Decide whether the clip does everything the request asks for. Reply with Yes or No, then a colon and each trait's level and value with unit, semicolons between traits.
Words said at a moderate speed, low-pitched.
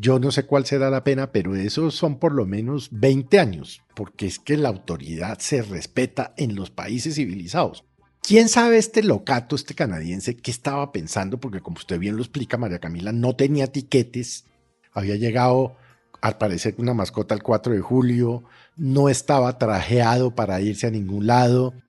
Yes: average, 175 wpm; low, 125 Hz